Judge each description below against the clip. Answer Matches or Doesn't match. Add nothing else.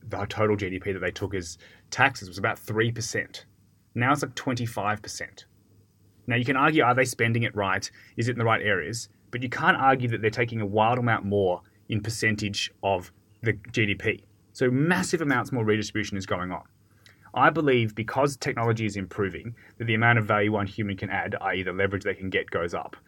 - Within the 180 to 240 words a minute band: Matches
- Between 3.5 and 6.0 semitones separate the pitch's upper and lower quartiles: Doesn't match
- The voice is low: Matches